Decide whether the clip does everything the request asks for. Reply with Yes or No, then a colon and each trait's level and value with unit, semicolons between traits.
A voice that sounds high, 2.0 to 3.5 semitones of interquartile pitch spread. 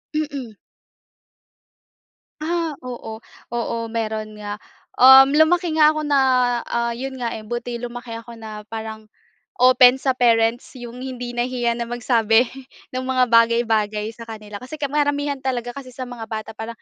Yes: high, 240 Hz; average, 2.7 semitones